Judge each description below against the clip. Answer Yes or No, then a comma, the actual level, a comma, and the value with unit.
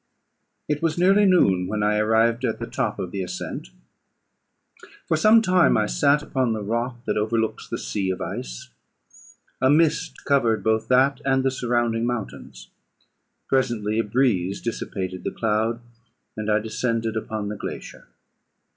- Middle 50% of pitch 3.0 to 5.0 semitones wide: Yes, average, 4.0 semitones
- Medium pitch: No, low, 115 Hz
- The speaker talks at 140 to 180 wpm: Yes, average, 155 wpm